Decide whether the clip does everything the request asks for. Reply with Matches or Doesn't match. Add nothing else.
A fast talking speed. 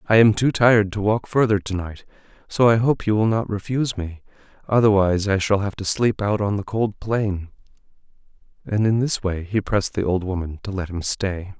Matches